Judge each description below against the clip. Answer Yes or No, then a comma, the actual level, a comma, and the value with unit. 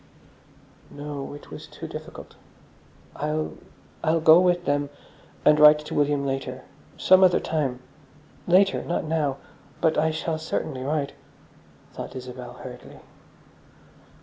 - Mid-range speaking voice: Yes, medium, 150 Hz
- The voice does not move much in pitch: Yes, narrow, 2.3 semitones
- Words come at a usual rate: No, slow, 120 wpm